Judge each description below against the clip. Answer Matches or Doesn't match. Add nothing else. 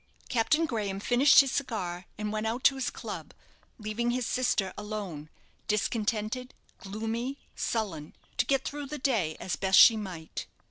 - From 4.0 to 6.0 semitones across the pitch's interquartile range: Matches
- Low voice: Doesn't match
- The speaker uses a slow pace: Doesn't match